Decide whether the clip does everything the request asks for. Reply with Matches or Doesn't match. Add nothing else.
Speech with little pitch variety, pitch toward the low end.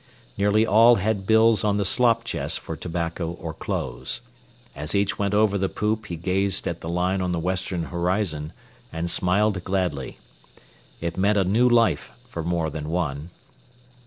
Doesn't match